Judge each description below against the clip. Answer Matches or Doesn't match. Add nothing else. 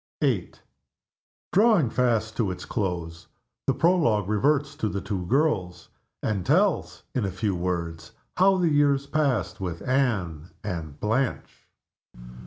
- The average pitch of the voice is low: Matches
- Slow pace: Matches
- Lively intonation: Matches